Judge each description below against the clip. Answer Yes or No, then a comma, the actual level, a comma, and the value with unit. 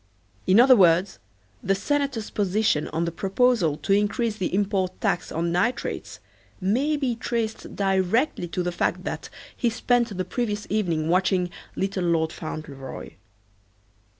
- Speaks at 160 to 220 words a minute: No, average, 140 wpm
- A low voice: No, high, 195 Hz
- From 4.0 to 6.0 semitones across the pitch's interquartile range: Yes, average, 4.5 semitones